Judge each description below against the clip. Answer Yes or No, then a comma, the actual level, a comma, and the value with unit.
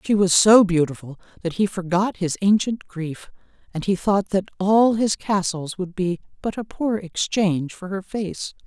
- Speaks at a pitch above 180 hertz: Yes, high, 190 Hz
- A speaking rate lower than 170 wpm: No, average, 180 wpm